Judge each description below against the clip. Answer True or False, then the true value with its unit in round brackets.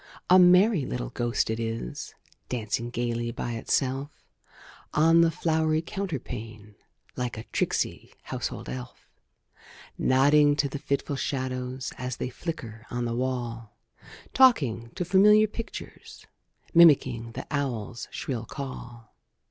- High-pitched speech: False (130 Hz)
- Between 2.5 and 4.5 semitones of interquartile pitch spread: False (5.1 semitones)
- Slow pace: True (120 wpm)